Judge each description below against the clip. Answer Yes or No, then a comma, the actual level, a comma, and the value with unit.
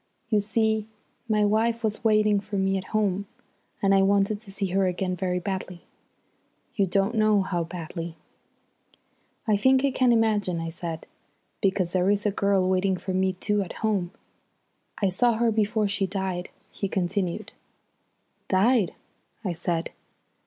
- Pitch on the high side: Yes, high, 195 Hz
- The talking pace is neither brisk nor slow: Yes, average, 155 wpm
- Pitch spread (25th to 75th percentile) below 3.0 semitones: Yes, narrow, 2.5 semitones